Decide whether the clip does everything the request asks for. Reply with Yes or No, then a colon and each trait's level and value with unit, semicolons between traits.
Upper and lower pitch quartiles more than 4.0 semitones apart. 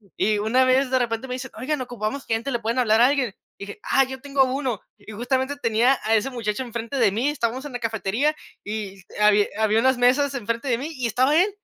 No: average, 3.2 semitones